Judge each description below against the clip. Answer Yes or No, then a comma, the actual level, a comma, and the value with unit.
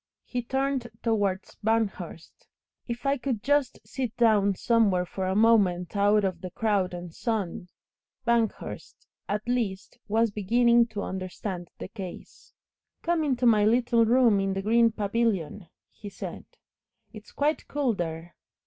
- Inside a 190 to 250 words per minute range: No, average, 145 wpm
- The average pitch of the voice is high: Yes, high, 215 Hz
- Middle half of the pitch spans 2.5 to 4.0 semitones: Yes, average, 3.7 semitones